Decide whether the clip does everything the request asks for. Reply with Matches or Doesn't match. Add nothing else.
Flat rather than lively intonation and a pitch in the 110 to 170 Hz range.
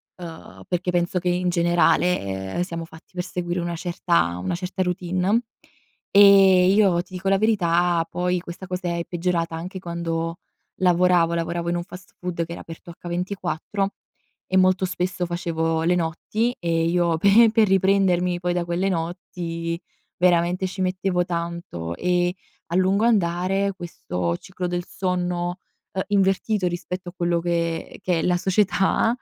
Doesn't match